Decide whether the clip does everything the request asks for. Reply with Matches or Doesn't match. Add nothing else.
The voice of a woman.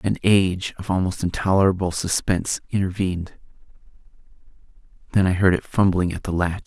Doesn't match